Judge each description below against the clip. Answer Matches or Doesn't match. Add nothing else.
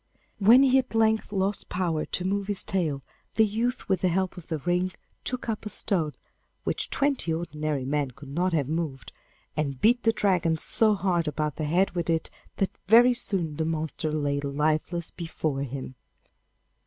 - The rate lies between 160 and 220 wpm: Matches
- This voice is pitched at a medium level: Matches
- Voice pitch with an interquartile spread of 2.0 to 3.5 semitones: Doesn't match